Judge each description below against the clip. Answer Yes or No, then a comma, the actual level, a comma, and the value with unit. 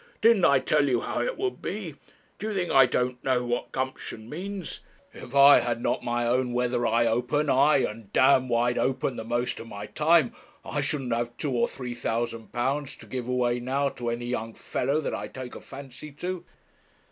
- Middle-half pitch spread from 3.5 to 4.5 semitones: No, average, 2.9 semitones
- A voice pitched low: Yes, low, 125 Hz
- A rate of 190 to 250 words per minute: Yes, fast, 205 wpm